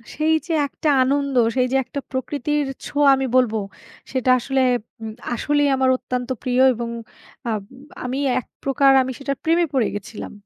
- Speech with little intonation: Yes, narrow, 2.3 semitones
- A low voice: No, very high, 265 Hz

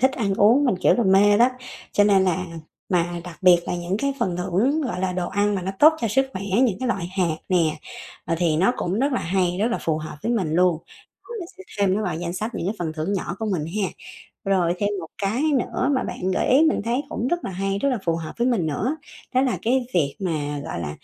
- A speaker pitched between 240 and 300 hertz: No, high, 190 Hz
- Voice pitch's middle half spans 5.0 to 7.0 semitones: Yes, average, 5.3 semitones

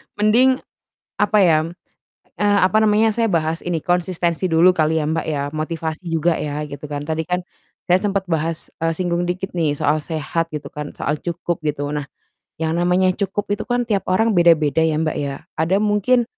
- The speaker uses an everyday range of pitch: Yes, average, 3.6 semitones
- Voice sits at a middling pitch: Yes, medium, 170 Hz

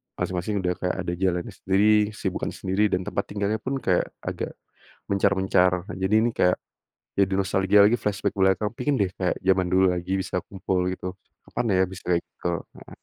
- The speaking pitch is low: Yes, very low, 95 Hz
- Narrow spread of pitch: Yes, narrow, 2.0 semitones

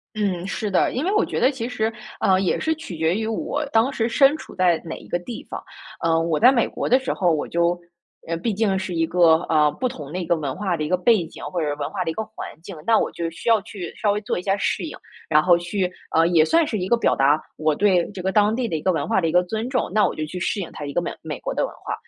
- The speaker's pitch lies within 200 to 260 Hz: No, medium, 185 Hz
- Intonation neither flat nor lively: Yes, average, 5.0 semitones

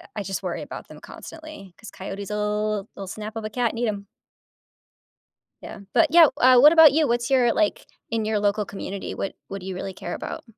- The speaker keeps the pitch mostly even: No, average, 3.6 semitones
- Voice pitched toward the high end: Yes, high, 215 Hz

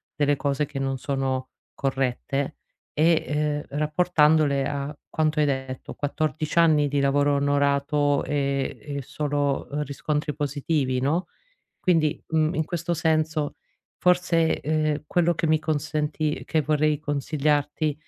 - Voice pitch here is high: No, medium, 150 Hz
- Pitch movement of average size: No, narrow, 1.7 semitones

